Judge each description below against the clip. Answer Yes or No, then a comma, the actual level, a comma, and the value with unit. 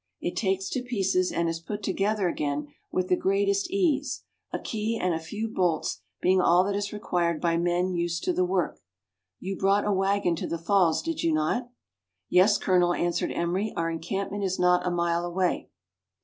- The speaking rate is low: No, fast, 205 wpm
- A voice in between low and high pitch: Yes, medium, 180 Hz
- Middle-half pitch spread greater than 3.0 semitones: No, average, 2.7 semitones